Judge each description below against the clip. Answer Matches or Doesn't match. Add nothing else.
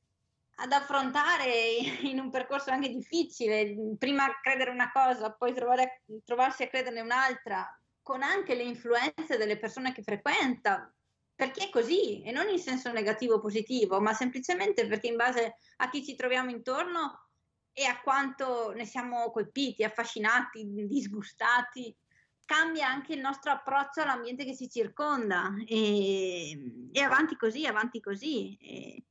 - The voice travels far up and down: Doesn't match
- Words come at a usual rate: Matches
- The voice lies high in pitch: Matches